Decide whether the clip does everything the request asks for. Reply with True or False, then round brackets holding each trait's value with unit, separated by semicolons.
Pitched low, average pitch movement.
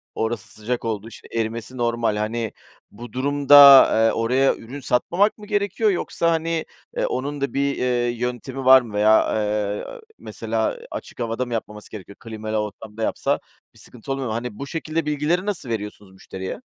True (120 Hz; 4.3 semitones)